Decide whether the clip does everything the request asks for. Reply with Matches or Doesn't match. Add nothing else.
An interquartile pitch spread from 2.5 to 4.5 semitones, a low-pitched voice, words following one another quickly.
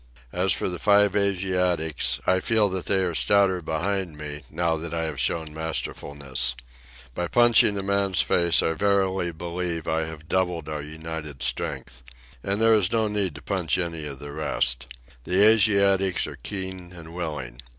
Doesn't match